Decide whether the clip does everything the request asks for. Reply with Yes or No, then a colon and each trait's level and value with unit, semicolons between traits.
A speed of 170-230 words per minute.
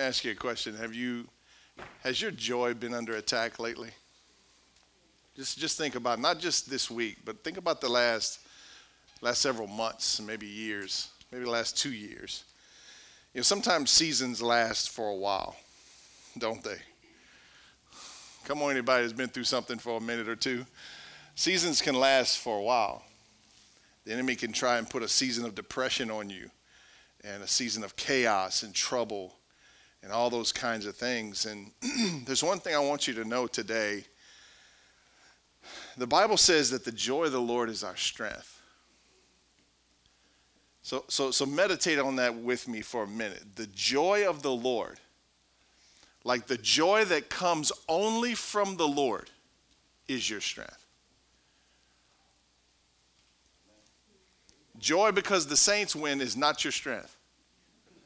No: average, 155 wpm